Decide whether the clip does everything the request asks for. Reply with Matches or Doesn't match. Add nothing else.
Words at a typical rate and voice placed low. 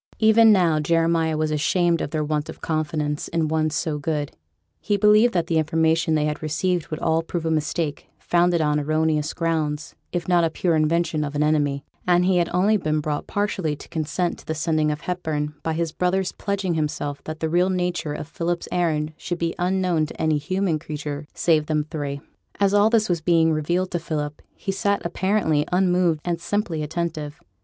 Doesn't match